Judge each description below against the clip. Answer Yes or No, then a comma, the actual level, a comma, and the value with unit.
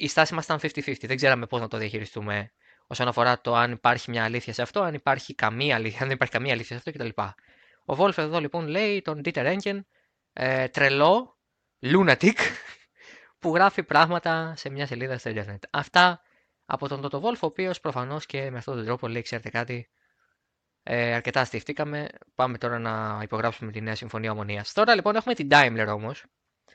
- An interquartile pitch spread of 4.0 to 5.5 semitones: Yes, average, 5.2 semitones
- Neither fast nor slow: No, fast, 190 wpm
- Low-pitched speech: Yes, low, 130 Hz